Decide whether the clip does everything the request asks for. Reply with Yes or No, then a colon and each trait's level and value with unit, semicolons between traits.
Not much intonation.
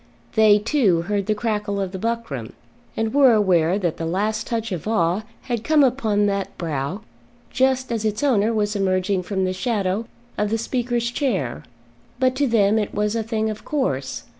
No: average, 3.4 semitones